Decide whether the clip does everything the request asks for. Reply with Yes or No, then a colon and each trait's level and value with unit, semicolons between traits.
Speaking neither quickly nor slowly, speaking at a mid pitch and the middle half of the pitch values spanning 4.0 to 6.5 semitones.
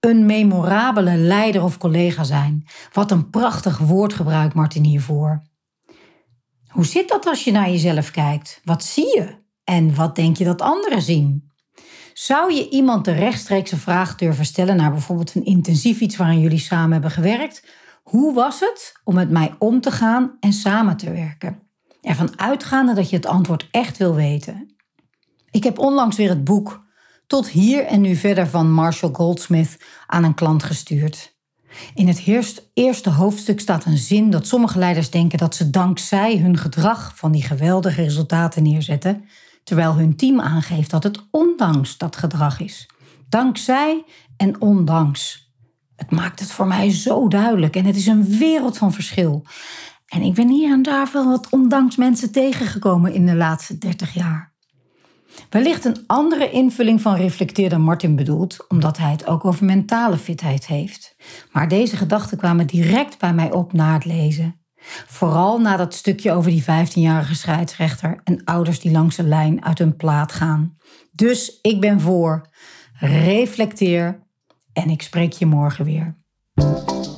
Yes: average, 165 wpm; medium, 180 Hz; average, 5.1 semitones